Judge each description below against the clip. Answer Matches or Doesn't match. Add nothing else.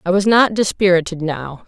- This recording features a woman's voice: Matches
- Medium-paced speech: Matches